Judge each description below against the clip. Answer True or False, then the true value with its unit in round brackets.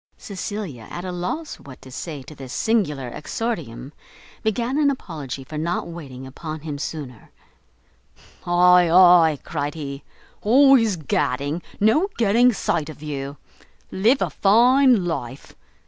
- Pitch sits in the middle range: True (170 Hz)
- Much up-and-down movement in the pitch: True (7.2 semitones)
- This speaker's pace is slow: True (130 wpm)